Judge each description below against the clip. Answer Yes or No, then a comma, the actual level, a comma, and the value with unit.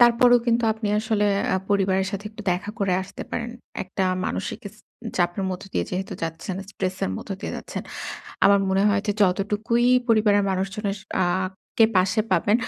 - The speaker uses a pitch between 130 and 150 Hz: No, high, 200 Hz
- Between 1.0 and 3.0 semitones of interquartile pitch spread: Yes, narrow, 2.4 semitones